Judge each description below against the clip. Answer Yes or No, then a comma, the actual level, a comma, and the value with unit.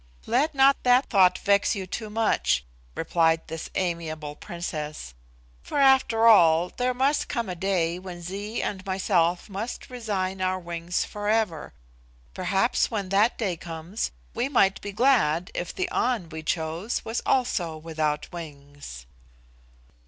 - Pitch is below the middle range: No, medium, 185 Hz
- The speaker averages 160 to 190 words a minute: No, average, 140 wpm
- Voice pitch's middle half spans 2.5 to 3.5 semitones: No, average, 5.3 semitones